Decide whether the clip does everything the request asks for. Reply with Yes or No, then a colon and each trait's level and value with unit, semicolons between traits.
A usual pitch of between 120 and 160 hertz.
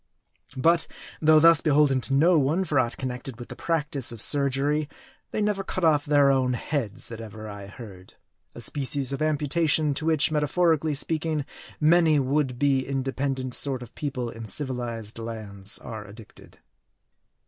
Yes: medium, 140 Hz